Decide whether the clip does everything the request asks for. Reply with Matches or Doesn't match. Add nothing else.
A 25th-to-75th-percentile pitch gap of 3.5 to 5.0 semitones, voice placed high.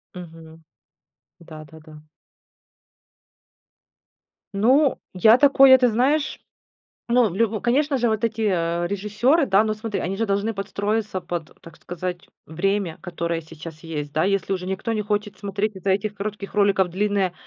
Matches